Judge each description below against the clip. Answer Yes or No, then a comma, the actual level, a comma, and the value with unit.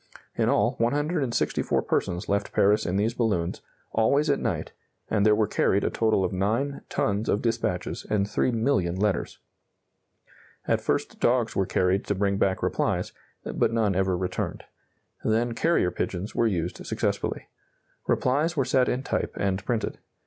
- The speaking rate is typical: Yes, average, 155 wpm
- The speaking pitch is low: Yes, low, 105 Hz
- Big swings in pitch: No, average, 3.8 semitones